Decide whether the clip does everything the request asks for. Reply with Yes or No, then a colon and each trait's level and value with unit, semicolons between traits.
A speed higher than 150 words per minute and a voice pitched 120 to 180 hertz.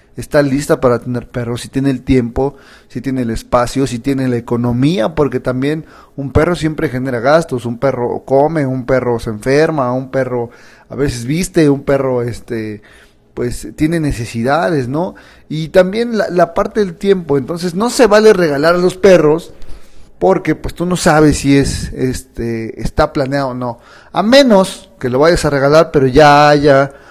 Yes: average, 175 wpm; medium, 140 Hz